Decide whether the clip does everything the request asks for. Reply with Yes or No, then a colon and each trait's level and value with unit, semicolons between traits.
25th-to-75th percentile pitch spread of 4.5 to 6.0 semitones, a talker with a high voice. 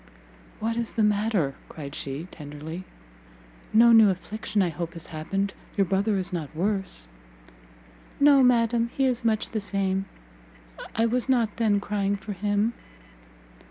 No: average, 3.9 semitones; high, 205 Hz